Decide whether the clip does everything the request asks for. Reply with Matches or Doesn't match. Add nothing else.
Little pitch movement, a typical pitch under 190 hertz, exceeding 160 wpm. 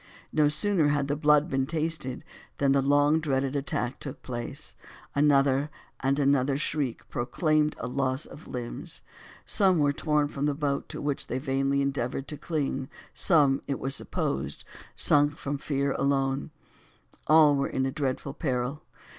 Doesn't match